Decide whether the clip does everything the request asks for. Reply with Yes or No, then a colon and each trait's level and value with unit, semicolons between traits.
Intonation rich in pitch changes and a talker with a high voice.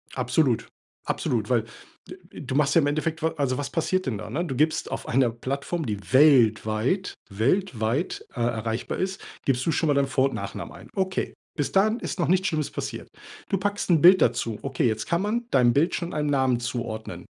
No: wide, 5.9 semitones; medium, 140 Hz